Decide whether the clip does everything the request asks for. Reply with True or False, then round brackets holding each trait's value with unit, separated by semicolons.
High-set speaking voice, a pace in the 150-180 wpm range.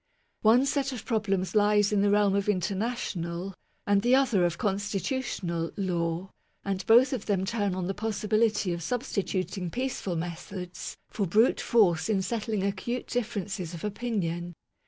True (200 Hz; 155 wpm)